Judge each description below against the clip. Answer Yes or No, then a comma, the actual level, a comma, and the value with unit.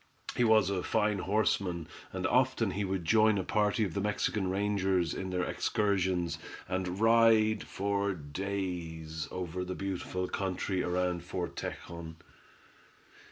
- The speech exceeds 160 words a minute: No, slow, 135 wpm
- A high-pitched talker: No, very low, 95 Hz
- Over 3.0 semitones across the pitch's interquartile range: No, narrow, 2.5 semitones